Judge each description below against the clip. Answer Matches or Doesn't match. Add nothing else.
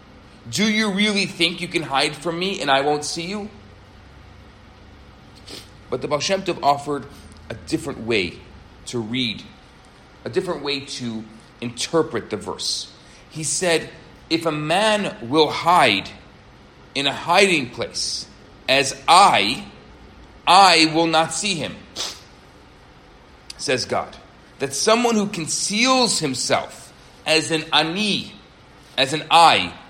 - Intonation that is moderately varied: Doesn't match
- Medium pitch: Matches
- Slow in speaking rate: Matches